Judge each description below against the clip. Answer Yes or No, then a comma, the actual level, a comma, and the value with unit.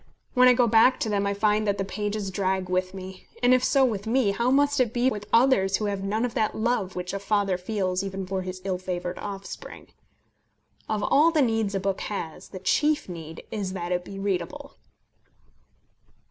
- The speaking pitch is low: No, high, 200 Hz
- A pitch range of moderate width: Yes, average, 3.5 semitones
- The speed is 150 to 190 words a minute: No, fast, 205 wpm